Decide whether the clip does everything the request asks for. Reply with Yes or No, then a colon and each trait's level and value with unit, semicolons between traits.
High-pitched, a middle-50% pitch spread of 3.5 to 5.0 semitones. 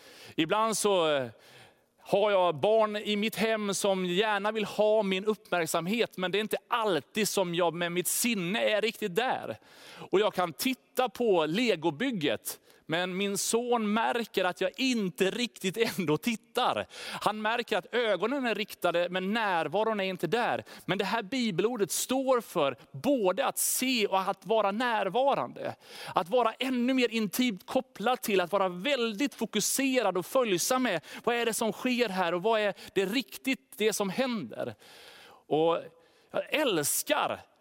Yes: high, 215 Hz; average, 4.1 semitones